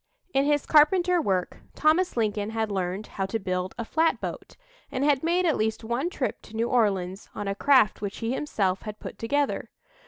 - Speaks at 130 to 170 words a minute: No, average, 190 wpm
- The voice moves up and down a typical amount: No, wide, 6.5 semitones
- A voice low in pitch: No, high, 225 Hz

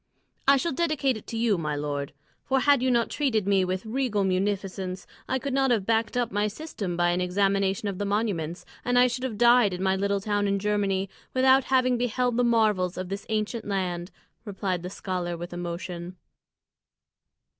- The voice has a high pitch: Yes, high, 205 Hz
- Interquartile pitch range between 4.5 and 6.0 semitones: Yes, average, 4.8 semitones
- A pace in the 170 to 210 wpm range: Yes, average, 190 wpm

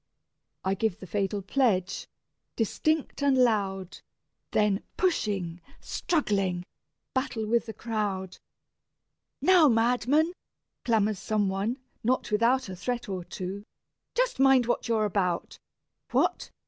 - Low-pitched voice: No, high, 215 Hz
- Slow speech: Yes, slow, 115 wpm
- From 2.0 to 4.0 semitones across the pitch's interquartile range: No, average, 4.6 semitones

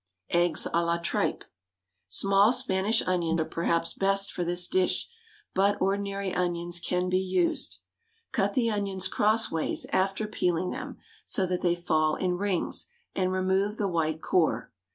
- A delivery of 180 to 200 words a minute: No, average, 155 wpm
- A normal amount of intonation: No, narrow, 2.3 semitones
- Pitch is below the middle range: No, medium, 185 Hz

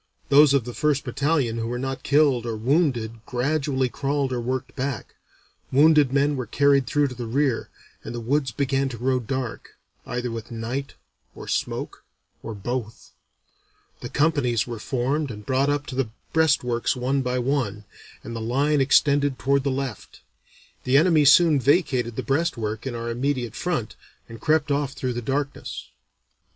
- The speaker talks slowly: No, average, 165 wpm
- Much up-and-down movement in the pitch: No, average, 3.0 semitones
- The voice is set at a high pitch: No, low, 130 Hz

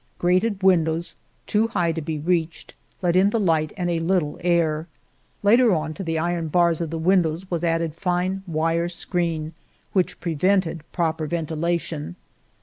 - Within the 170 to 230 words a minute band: No, average, 155 wpm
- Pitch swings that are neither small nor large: No, narrow, 2.1 semitones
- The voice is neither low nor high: Yes, medium, 170 Hz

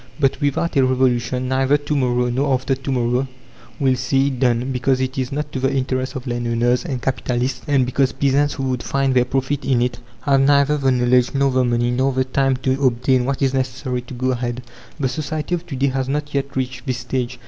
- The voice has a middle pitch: No, low, 130 Hz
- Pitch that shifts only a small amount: Yes, narrow, 1.5 semitones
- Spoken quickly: Yes, fast, 225 wpm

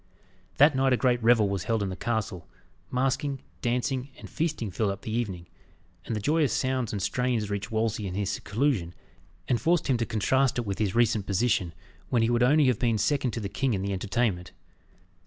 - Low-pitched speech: Yes, low, 115 Hz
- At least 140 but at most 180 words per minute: No, fast, 205 wpm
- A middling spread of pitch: Yes, average, 4.2 semitones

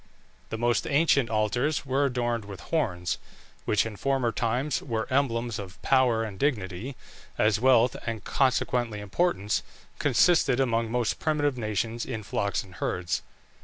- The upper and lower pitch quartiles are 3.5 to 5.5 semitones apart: Yes, average, 3.8 semitones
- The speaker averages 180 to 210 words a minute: No, average, 140 wpm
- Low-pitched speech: Yes, low, 115 Hz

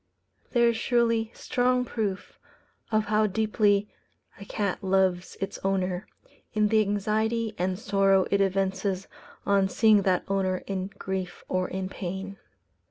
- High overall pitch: Yes, high, 195 Hz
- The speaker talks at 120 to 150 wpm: Yes, slow, 135 wpm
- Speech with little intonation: Yes, narrow, 2.3 semitones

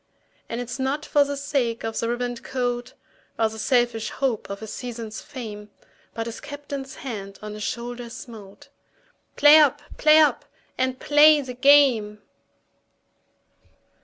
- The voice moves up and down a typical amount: Yes, average, 3.9 semitones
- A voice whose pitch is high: Yes, high, 245 Hz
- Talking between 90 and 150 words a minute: Yes, average, 145 wpm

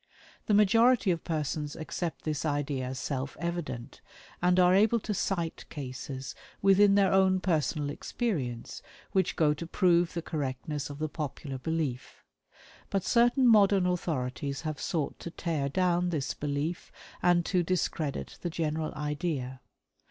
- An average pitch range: Yes, average, 4.2 semitones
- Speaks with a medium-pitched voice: Yes, medium, 165 Hz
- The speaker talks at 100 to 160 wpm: Yes, average, 145 wpm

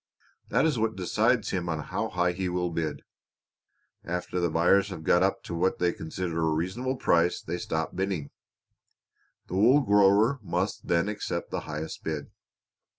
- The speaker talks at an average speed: Yes, average, 165 wpm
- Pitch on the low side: Yes, very low, 90 Hz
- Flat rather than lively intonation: No, average, 3.3 semitones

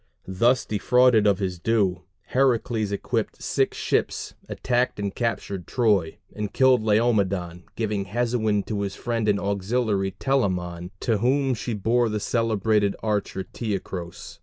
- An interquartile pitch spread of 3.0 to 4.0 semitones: Yes, average, 3.3 semitones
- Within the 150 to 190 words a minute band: No, slow, 135 wpm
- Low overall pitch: Yes, low, 105 Hz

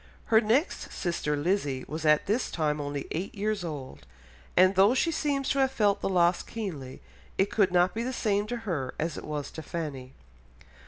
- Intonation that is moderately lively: No, wide, 6.2 semitones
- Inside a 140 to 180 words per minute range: No, average, 195 wpm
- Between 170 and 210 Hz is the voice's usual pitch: Yes, medium, 185 Hz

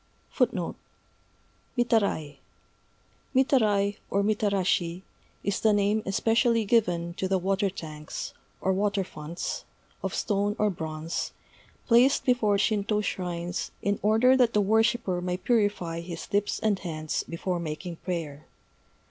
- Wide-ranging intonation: No, average, 3.7 semitones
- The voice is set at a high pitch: Yes, high, 200 Hz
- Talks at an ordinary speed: No, slow, 120 wpm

